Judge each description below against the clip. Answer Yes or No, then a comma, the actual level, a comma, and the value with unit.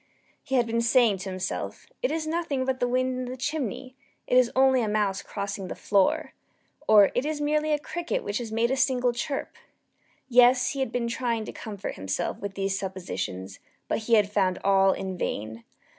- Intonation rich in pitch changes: No, average, 4.7 semitones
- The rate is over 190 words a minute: Yes, average, 200 wpm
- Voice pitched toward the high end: Yes, high, 235 Hz